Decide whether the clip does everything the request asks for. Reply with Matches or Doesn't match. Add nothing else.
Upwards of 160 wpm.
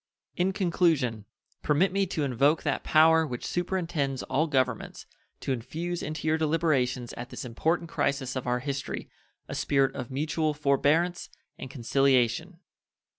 Doesn't match